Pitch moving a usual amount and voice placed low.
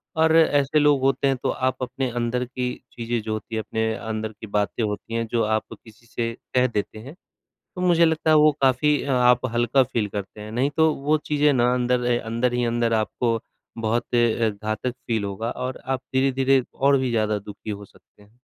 Yes: average, 3.2 semitones; low, 120 Hz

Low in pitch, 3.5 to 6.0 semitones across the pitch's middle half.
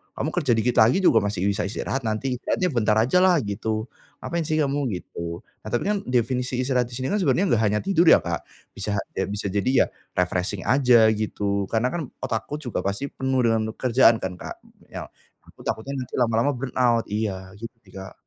Yes: low, 115 Hz; average, 4.0 semitones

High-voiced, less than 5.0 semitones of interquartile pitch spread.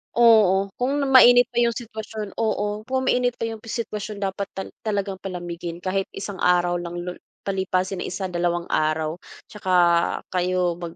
Yes: high, 195 Hz; average, 3.7 semitones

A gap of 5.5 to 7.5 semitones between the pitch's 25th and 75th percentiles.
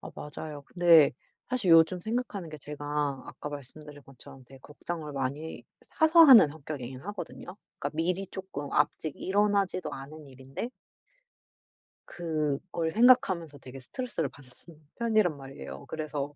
No: average, 5.1 semitones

